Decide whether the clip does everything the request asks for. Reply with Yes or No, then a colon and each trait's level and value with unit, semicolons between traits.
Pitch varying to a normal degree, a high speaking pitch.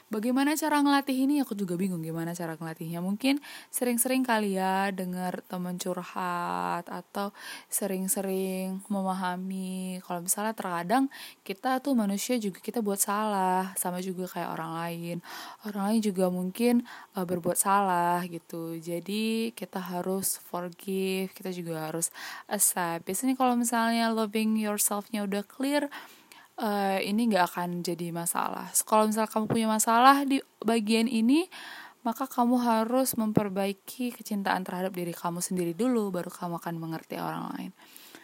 Yes: average, 4.3 semitones; high, 200 Hz